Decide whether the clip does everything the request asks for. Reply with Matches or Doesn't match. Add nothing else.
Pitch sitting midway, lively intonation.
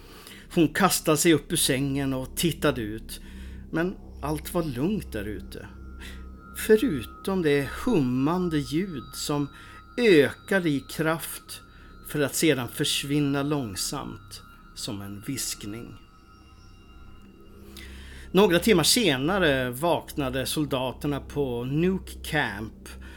Doesn't match